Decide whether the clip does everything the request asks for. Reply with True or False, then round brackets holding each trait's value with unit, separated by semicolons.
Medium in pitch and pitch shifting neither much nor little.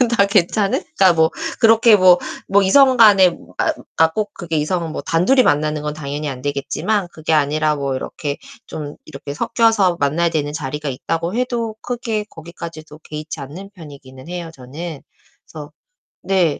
True (165 Hz; 4.8 semitones)